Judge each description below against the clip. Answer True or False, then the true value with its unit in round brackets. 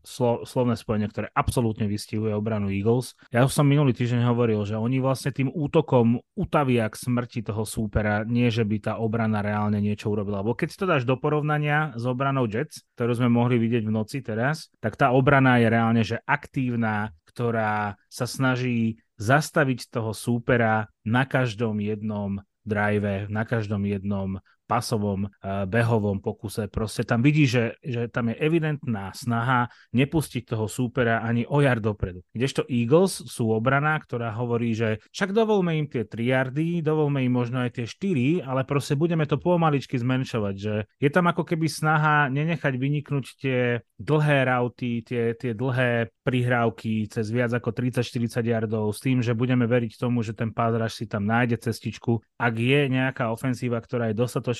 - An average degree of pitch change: True (3.2 semitones)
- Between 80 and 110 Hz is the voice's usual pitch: False (120 Hz)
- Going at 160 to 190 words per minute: True (165 wpm)